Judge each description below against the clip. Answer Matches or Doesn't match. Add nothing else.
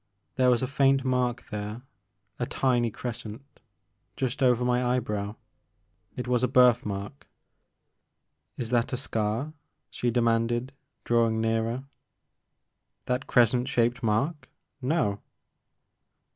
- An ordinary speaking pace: Doesn't match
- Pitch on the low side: Matches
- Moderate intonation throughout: Doesn't match